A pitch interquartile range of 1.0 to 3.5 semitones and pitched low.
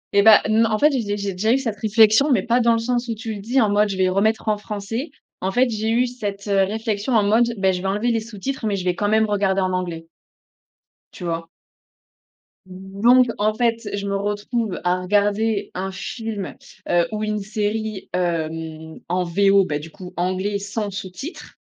No: average, 2.8 semitones; high, 205 Hz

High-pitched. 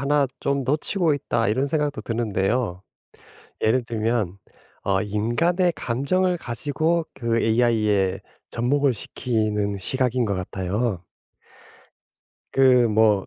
No: low, 120 Hz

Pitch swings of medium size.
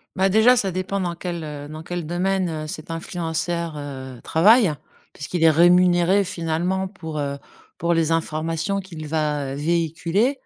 Yes: average, 3.0 semitones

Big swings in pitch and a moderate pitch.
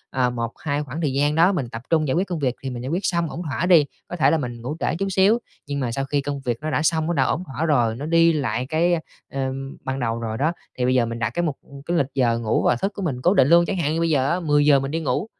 No: average, 4.6 semitones; medium, 145 Hz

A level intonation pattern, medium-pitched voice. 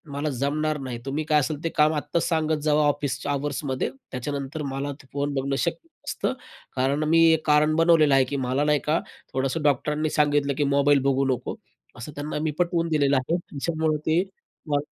Yes: narrow, 1.9 semitones; medium, 150 Hz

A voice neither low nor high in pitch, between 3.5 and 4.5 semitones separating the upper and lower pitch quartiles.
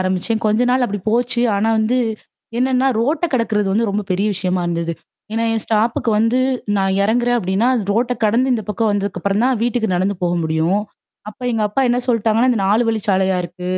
No: high, 215 Hz; average, 3.8 semitones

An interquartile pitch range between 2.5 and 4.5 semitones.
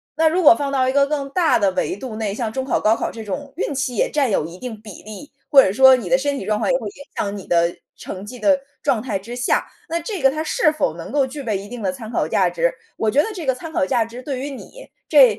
No: average, 5.0 semitones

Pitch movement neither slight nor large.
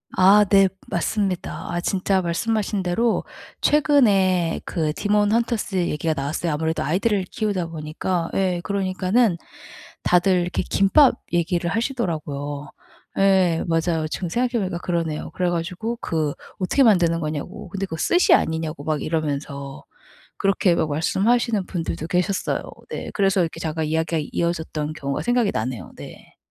Yes: average, 3.8 semitones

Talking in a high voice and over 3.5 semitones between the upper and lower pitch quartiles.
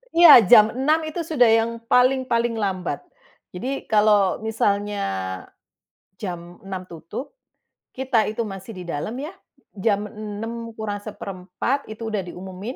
Yes: high, 215 Hz; average, 4.1 semitones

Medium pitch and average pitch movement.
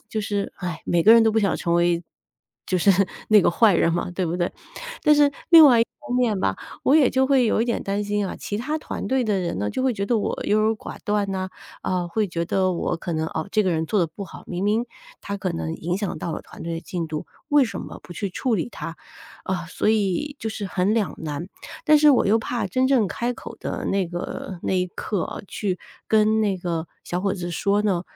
No: high, 200 Hz; average, 4.2 semitones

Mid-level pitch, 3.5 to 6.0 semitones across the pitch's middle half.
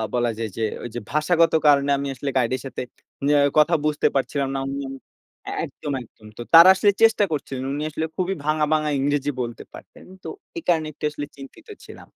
No: medium, 145 Hz; average, 2.7 semitones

